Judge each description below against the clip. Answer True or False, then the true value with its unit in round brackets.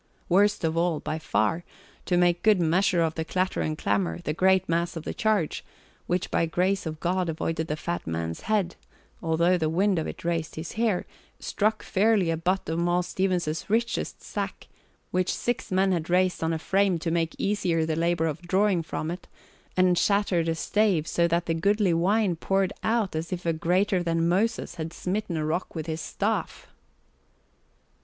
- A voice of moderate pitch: True (175 Hz)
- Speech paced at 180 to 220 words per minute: True (190 wpm)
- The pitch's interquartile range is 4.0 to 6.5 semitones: False (2.8 semitones)